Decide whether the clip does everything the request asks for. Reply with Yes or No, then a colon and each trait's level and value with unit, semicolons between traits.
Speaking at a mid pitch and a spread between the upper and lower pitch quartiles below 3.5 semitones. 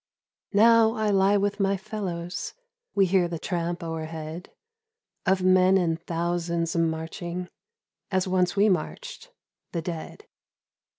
Yes: medium, 180 Hz; average, 2.7 semitones